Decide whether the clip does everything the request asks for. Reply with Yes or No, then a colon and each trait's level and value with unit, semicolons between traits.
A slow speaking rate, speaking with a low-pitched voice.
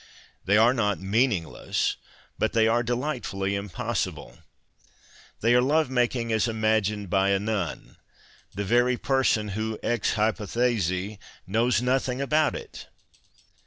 Yes: slow, 125 wpm; low, 110 Hz